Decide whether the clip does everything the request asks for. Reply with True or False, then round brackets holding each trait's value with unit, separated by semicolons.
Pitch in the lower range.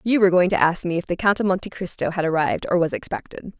False (180 Hz)